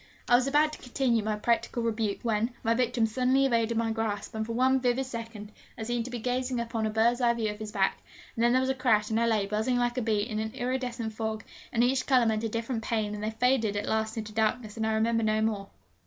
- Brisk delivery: Yes, fast, 255 wpm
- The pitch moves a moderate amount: No, narrow, 2.1 semitones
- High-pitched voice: Yes, high, 230 Hz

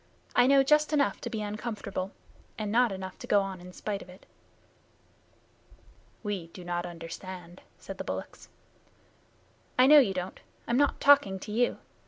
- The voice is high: Yes, high, 205 Hz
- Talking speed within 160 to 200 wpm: Yes, average, 165 wpm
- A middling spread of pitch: Yes, average, 5.0 semitones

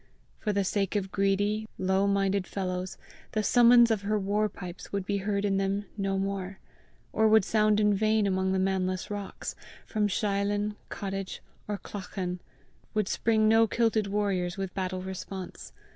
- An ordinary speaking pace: Yes, average, 160 wpm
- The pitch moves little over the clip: Yes, narrow, 1.7 semitones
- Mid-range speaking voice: No, high, 200 Hz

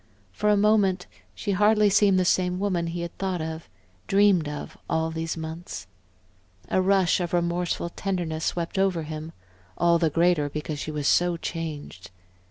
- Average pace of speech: Yes, average, 165 wpm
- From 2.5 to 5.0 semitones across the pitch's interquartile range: Yes, average, 2.9 semitones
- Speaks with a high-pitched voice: No, medium, 175 Hz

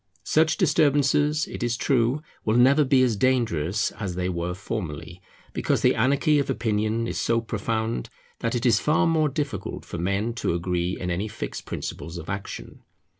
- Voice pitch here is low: Yes, low, 115 Hz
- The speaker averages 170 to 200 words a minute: Yes, average, 175 wpm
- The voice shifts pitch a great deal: Yes, wide, 6.6 semitones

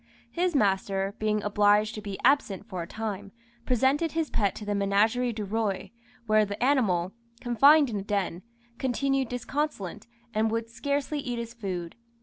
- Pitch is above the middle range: Yes, high, 215 Hz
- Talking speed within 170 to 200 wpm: No, average, 160 wpm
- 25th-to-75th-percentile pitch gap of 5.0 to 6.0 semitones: No, average, 4.2 semitones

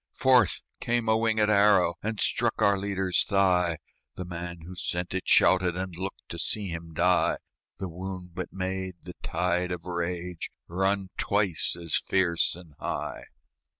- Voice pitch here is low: Yes, very low, 90 Hz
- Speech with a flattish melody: Yes, narrow, 2.0 semitones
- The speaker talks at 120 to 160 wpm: Yes, average, 155 wpm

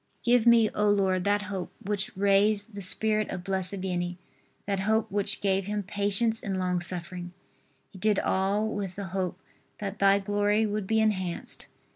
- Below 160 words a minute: No, average, 170 wpm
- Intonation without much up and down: Yes, narrow, 1.9 semitones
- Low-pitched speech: No, high, 200 Hz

